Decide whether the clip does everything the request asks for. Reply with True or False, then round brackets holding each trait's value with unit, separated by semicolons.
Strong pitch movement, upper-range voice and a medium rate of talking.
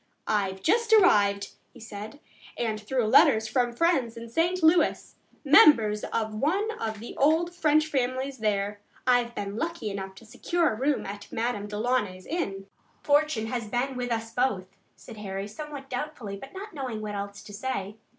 True (5.9 semitones; 235 Hz; 170 wpm)